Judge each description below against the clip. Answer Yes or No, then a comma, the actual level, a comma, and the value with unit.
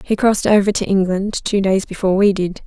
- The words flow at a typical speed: No, fast, 225 wpm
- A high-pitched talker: Yes, high, 195 Hz